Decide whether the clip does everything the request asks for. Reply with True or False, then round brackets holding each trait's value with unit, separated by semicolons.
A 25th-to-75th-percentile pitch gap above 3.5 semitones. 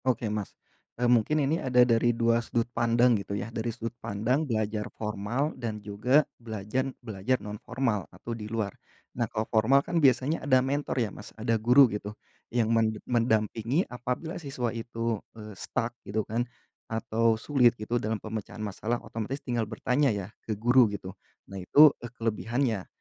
False (2.6 semitones)